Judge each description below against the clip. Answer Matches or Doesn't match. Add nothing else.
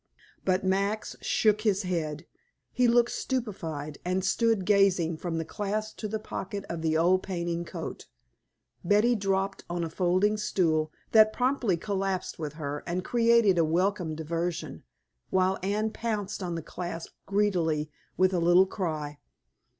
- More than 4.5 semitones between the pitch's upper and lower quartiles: Doesn't match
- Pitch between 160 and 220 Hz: Matches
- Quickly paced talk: Doesn't match